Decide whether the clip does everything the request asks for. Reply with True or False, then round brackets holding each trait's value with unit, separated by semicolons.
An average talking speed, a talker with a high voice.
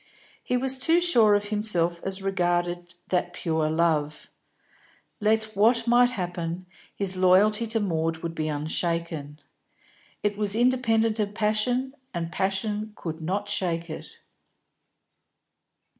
False (125 wpm; 195 Hz)